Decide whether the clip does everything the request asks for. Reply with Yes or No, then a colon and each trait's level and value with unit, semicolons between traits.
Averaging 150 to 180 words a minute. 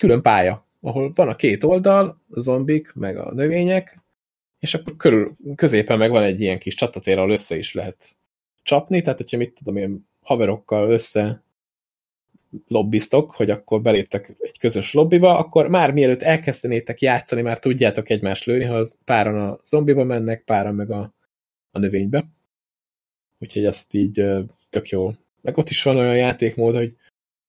Yes: fast, 155 wpm